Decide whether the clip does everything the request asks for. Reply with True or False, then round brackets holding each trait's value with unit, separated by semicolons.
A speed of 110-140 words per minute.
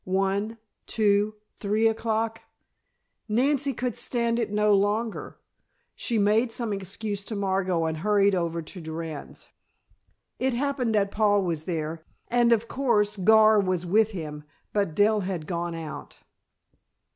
True (135 wpm)